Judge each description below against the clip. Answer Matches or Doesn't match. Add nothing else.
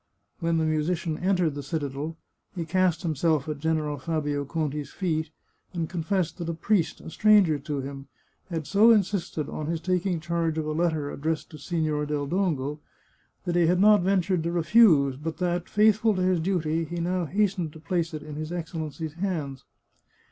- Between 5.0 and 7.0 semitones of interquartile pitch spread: Doesn't match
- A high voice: Doesn't match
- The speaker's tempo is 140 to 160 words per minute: Doesn't match